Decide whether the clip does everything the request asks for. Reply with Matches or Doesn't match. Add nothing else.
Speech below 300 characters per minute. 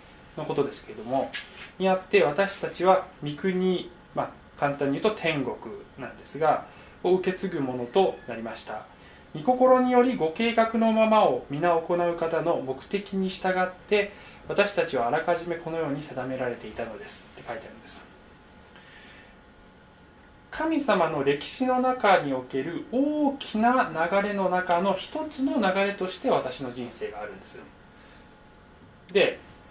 Matches